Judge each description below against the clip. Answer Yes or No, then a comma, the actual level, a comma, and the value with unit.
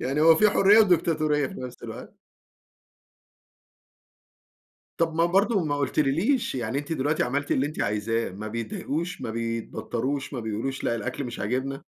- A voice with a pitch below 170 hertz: Yes, medium, 140 Hz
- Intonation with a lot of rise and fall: Yes, wide, 5.8 semitones